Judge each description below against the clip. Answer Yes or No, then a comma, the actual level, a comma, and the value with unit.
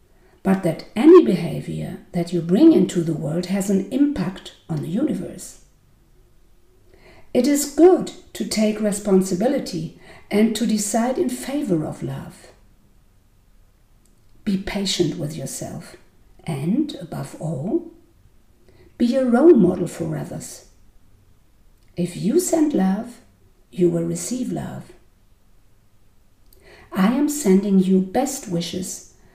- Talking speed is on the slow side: Yes, slow, 115 wpm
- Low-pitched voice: No, medium, 180 Hz